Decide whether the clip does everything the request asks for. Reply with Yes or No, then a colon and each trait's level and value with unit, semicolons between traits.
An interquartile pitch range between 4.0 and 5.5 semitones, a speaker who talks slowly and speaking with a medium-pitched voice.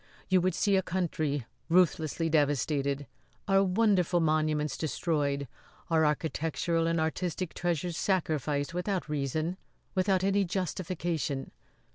No: average, 3.4 semitones; slow, 110 wpm; medium, 165 Hz